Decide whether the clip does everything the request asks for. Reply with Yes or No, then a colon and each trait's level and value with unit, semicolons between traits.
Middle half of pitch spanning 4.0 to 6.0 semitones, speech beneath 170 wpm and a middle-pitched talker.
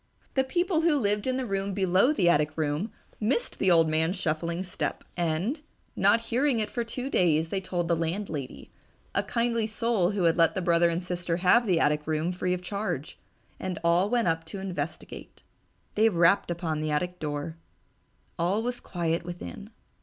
No: average, 4.5 semitones; average, 185 wpm; medium, 180 Hz